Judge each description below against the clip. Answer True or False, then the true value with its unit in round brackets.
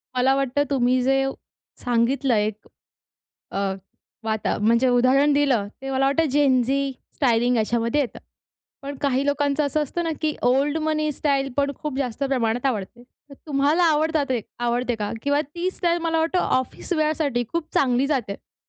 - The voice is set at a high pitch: True (275 Hz)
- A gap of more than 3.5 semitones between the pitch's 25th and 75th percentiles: False (3.1 semitones)